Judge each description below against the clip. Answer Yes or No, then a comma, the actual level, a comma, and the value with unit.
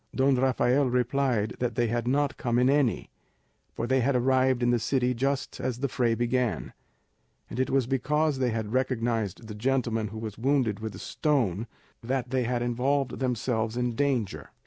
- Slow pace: No, average, 180 wpm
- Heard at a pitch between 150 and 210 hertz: No, low, 125 Hz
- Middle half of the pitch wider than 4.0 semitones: No, narrow, 2.4 semitones